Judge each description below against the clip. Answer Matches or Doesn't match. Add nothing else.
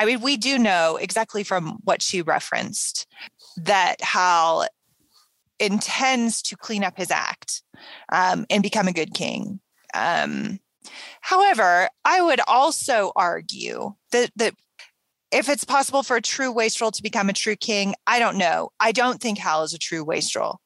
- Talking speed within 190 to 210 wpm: Doesn't match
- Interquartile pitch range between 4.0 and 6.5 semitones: Matches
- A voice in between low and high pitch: Doesn't match